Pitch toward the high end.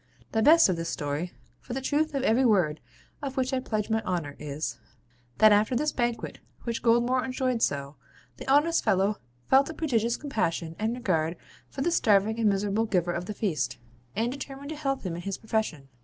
Yes: high, 220 Hz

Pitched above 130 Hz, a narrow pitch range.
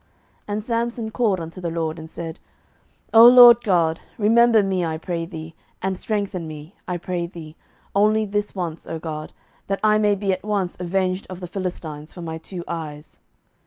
No: medium, 185 Hz; average, 4.1 semitones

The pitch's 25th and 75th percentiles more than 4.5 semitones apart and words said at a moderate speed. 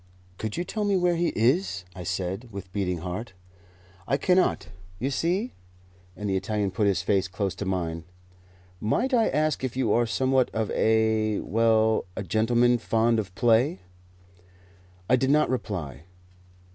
Yes: wide, 5.4 semitones; average, 160 wpm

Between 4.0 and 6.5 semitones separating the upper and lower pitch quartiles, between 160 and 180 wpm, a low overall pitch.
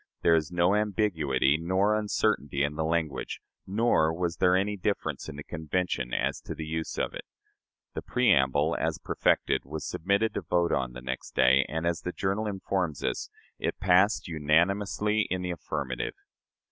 Yes: average, 4.7 semitones; average, 170 wpm; very low, 85 Hz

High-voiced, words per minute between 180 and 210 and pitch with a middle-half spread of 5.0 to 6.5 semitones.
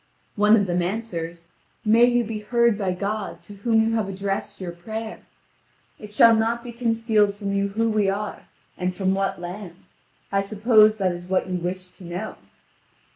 No: high, 205 Hz; average, 185 wpm; average, 3.0 semitones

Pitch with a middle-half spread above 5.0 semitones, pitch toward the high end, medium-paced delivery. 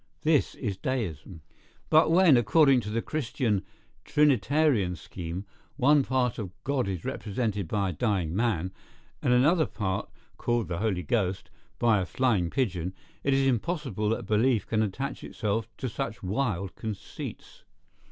No: wide, 5.5 semitones; low, 115 Hz; average, 145 wpm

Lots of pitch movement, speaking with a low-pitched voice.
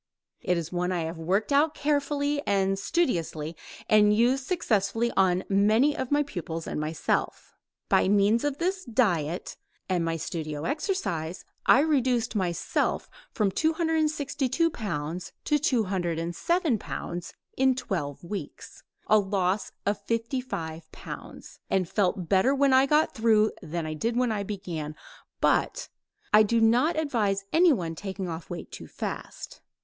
No: wide, 7.4 semitones; high, 210 Hz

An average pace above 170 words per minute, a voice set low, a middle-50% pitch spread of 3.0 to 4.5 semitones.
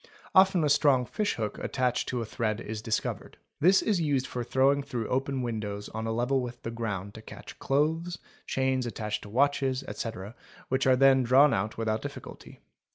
Yes: average, 185 wpm; low, 125 Hz; average, 3.7 semitones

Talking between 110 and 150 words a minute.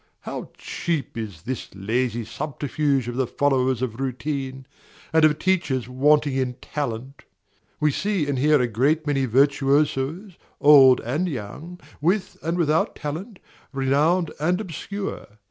Yes: slow, 135 wpm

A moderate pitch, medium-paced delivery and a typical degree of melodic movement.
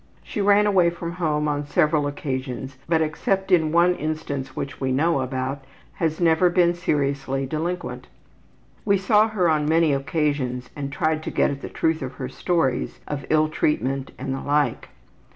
Yes: medium, 155 Hz; average, 170 wpm; average, 3.8 semitones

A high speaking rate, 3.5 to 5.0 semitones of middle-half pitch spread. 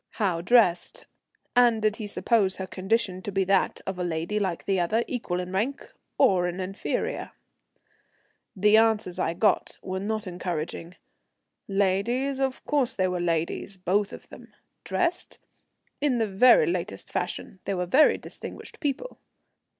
No: average, 150 wpm; average, 4.2 semitones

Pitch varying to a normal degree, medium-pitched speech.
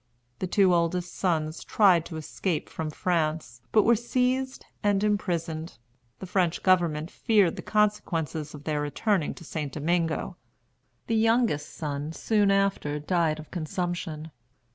Yes: average, 4.2 semitones; medium, 170 Hz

